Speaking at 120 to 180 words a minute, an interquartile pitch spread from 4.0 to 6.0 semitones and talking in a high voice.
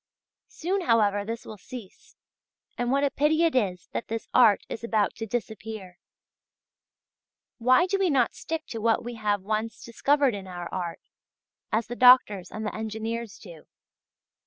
No: average, 160 wpm; average, 3.6 semitones; high, 225 Hz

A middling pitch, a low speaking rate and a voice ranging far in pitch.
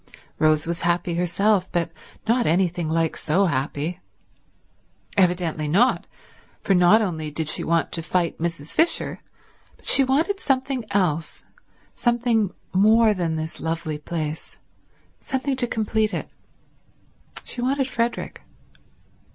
Yes: medium, 180 Hz; slow, 125 wpm; wide, 5.9 semitones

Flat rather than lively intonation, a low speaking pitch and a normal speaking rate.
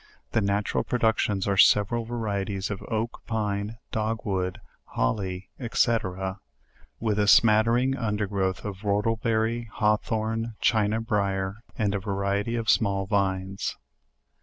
No: narrow, 2.3 semitones; low, 105 Hz; slow, 115 wpm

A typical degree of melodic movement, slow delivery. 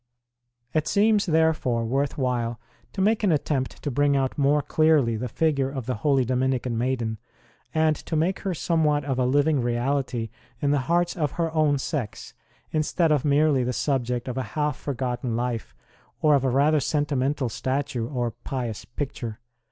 No: average, 3.6 semitones; average, 175 wpm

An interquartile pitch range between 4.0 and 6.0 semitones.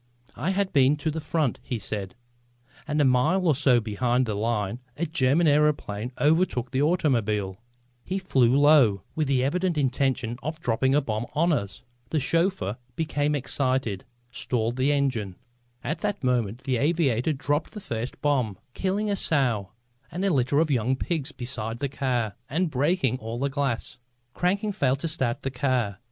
Yes: average, 4.6 semitones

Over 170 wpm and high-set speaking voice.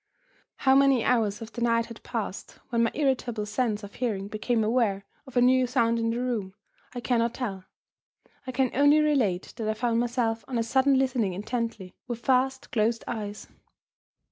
Yes: average, 180 wpm; high, 235 Hz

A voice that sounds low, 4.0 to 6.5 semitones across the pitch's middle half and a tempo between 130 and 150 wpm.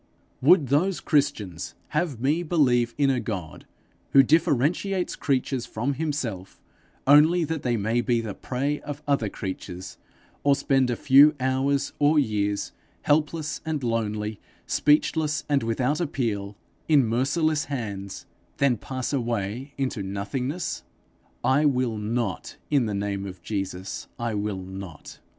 Yes: low, 130 Hz; wide, 5.6 semitones; slow, 135 wpm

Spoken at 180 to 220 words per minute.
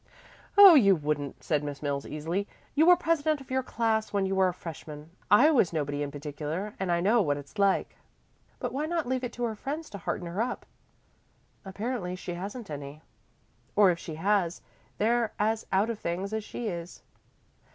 Yes: average, 195 wpm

